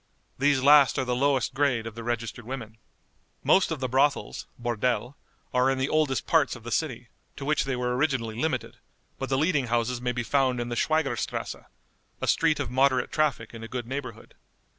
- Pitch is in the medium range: No, low, 130 Hz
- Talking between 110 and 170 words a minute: No, average, 200 wpm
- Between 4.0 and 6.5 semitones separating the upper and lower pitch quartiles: No, average, 2.8 semitones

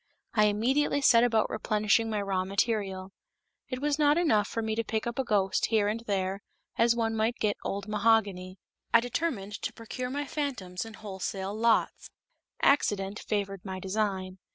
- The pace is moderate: Yes, average, 170 wpm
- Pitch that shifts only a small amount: No, average, 3.0 semitones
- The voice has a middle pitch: No, high, 215 Hz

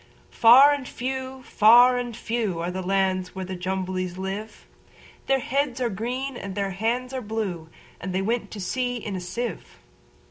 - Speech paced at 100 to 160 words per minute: Yes, average, 155 wpm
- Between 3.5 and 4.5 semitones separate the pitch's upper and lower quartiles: No, average, 4.9 semitones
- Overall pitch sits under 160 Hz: No, high, 220 Hz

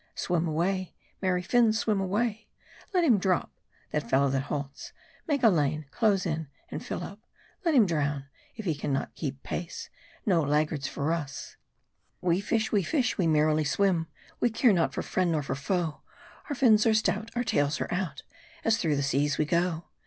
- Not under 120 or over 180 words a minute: No, average, 190 wpm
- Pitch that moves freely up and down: Yes, wide, 6.2 semitones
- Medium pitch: Yes, medium, 175 Hz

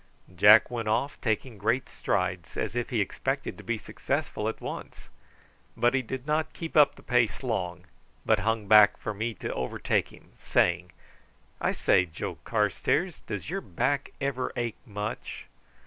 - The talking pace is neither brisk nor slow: Yes, average, 165 wpm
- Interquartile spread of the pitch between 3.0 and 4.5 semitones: Yes, average, 4.2 semitones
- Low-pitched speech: Yes, low, 110 Hz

